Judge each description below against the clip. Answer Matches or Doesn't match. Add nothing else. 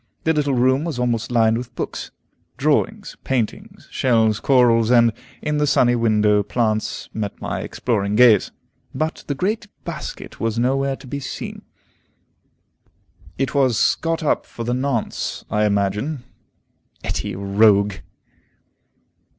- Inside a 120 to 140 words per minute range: Matches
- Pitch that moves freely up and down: Doesn't match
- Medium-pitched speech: Doesn't match